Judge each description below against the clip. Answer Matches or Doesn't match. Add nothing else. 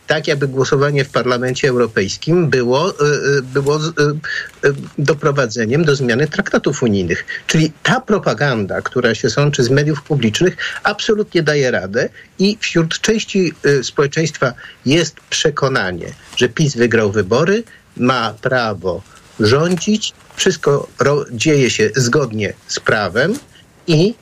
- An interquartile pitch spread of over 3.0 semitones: Matches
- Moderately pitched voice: Matches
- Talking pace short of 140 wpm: Matches